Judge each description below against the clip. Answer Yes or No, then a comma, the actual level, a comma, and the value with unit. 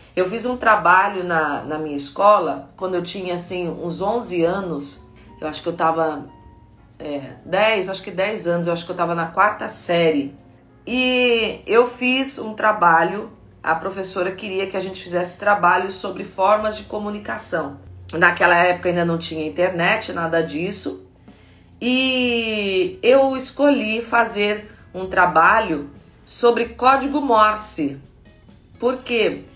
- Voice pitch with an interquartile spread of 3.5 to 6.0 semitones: Yes, average, 4.7 semitones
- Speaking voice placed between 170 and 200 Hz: Yes, medium, 185 Hz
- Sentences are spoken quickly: No, average, 140 wpm